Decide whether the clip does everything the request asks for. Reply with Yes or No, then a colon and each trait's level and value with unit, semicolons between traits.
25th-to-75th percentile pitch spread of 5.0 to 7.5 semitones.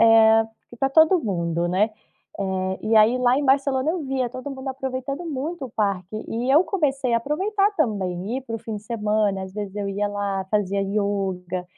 Yes: average, 5.3 semitones